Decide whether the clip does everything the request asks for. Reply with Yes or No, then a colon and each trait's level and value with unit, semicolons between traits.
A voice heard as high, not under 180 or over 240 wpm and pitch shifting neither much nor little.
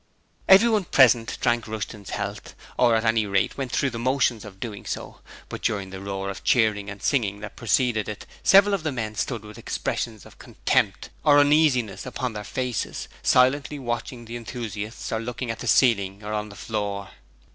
No: low, 115 Hz; average, 185 wpm; average, 3.5 semitones